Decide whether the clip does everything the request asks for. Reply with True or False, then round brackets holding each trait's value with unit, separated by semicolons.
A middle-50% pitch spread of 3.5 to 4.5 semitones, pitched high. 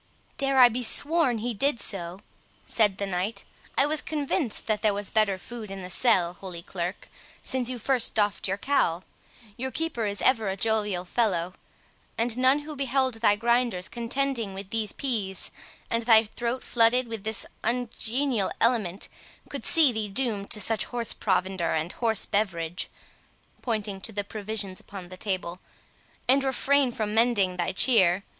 True (4.1 semitones; 220 Hz)